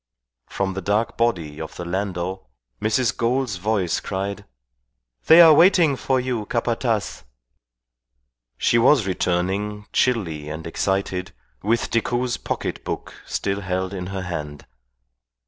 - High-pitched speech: No, low, 100 Hz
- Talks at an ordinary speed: No, slow, 125 wpm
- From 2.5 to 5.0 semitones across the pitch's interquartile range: Yes, average, 4.3 semitones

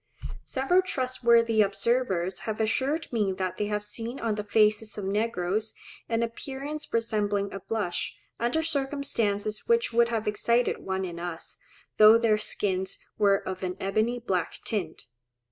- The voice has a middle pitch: No, high, 215 Hz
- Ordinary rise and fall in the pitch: Yes, average, 3.1 semitones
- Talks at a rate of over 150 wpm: No, average, 145 wpm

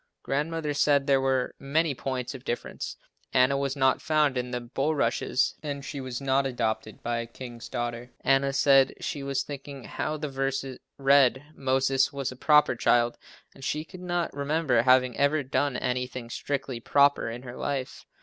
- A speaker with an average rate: Yes, average, 170 wpm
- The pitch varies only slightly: Yes, narrow, 2.0 semitones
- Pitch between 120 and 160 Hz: Yes, low, 135 Hz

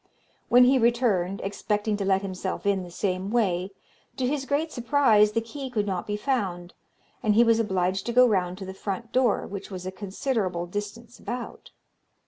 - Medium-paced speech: Yes, average, 185 wpm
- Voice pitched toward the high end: Yes, high, 210 Hz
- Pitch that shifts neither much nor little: Yes, average, 4.0 semitones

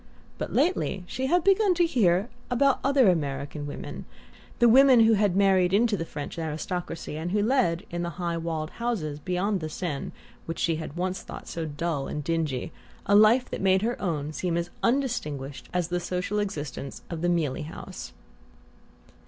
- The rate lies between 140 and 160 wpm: No, average, 175 wpm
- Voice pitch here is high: No, medium, 180 Hz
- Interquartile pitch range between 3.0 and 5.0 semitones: No, wide, 5.5 semitones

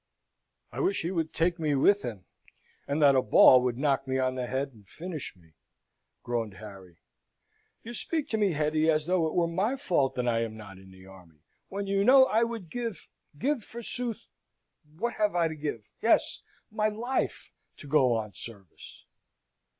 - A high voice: No, medium, 155 Hz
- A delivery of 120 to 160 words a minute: No, average, 185 wpm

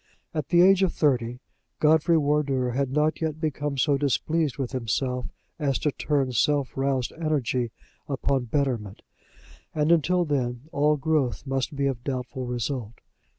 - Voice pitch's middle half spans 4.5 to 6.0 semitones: No, average, 3.1 semitones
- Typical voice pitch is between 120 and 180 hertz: Yes, medium, 140 Hz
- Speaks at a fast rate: No, average, 150 wpm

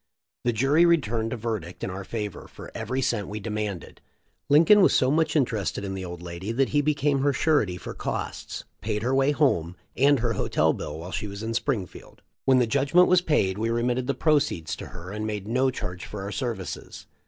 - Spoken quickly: Yes, fast, 210 wpm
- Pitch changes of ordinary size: No, wide, 5.7 semitones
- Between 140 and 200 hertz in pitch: No, low, 115 Hz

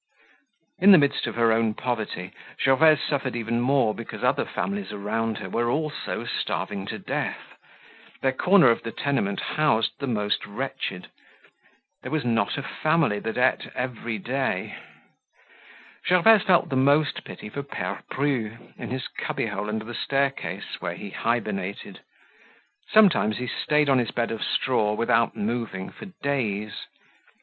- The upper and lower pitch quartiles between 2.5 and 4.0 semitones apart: No, average, 4.4 semitones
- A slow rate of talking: No, average, 150 wpm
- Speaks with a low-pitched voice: Yes, low, 120 Hz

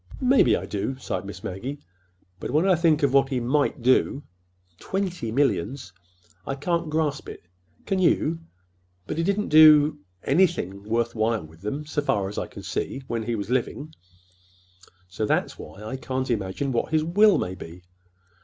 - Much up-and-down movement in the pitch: Yes, wide, 7.1 semitones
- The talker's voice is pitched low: Yes, low, 130 Hz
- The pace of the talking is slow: No, average, 165 wpm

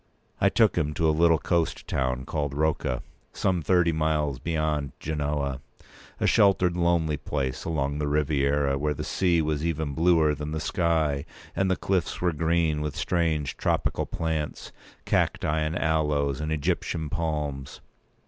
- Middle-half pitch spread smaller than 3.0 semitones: Yes, narrow, 2.4 semitones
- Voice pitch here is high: No, very low, 75 Hz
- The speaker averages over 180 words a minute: No, average, 150 wpm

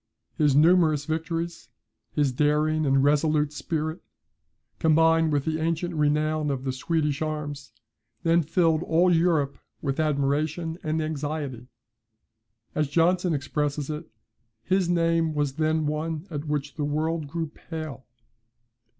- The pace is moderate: No, slow, 125 wpm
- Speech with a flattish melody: Yes, narrow, 1.9 semitones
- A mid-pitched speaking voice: Yes, medium, 155 Hz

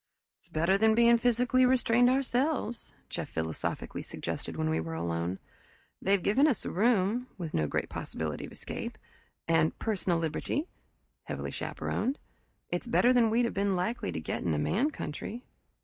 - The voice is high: Yes, high, 210 Hz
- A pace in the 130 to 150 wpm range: No, average, 165 wpm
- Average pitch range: No, wide, 7.6 semitones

